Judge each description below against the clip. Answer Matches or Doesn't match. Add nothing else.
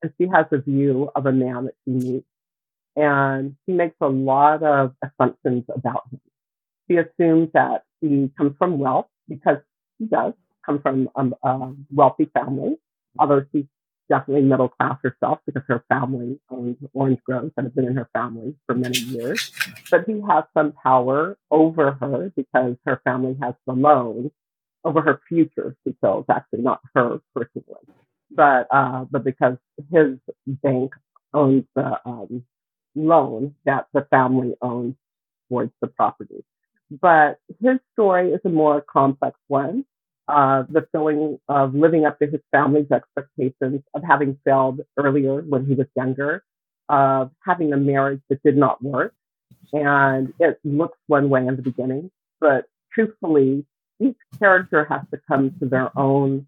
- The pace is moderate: Matches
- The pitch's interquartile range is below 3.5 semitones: Matches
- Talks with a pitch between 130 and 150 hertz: Matches